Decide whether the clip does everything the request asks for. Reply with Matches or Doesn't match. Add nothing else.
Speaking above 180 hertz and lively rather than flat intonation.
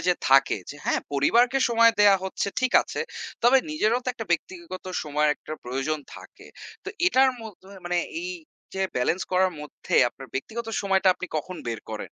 Matches